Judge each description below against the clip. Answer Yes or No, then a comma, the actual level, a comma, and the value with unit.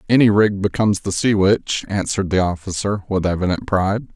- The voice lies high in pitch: No, low, 100 Hz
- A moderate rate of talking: Yes, average, 175 wpm